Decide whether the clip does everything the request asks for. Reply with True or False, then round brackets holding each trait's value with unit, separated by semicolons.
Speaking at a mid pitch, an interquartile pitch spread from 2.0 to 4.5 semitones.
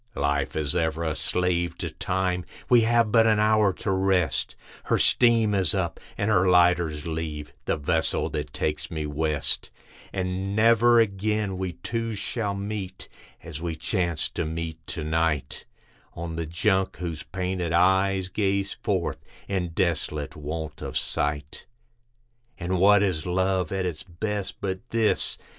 False (90 Hz; 3.5 semitones)